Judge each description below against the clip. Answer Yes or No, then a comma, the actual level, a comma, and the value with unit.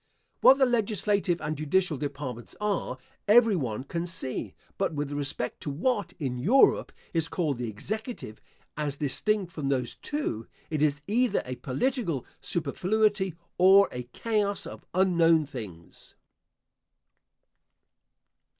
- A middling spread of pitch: No, wide, 7.0 semitones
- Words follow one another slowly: Yes, slow, 125 wpm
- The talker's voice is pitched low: No, medium, 165 Hz